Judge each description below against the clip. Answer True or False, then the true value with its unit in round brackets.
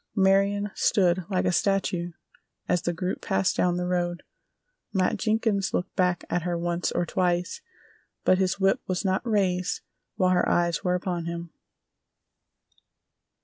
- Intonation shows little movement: True (1.7 semitones)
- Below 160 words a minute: True (145 wpm)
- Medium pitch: True (180 Hz)